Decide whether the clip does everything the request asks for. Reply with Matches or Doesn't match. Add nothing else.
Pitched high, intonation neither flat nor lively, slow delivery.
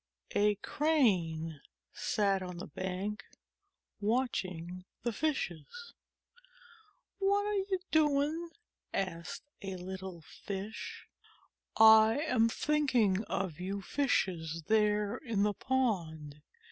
Doesn't match